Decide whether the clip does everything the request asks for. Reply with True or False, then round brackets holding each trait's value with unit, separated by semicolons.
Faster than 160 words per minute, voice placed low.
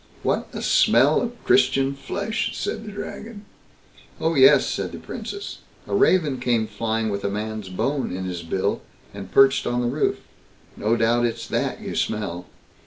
True (170 wpm; 120 Hz)